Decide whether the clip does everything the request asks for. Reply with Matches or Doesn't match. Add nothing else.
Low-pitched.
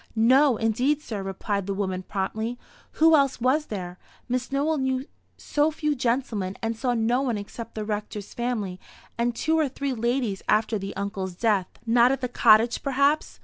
Doesn't match